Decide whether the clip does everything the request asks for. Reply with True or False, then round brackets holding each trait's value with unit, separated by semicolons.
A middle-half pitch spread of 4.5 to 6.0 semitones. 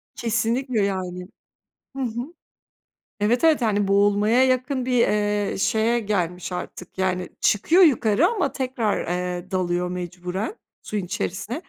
True (5.2 semitones)